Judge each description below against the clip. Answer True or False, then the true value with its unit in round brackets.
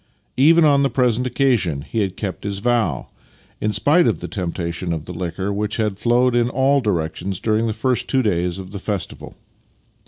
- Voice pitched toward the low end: True (105 Hz)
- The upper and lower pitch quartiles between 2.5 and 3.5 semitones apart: False (5.3 semitones)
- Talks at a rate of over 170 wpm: True (190 wpm)